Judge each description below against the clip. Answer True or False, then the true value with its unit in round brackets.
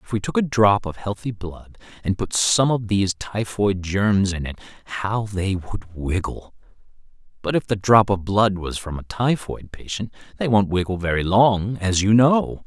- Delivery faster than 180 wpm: True (190 wpm)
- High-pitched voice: False (100 Hz)